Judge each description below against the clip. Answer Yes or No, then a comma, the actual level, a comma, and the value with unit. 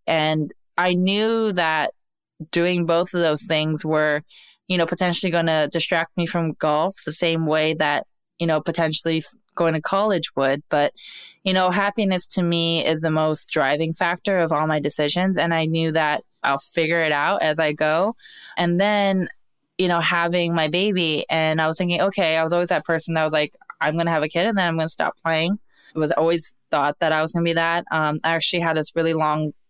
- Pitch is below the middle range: No, medium, 165 Hz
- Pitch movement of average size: No, narrow, 2.1 semitones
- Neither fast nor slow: No, fast, 215 wpm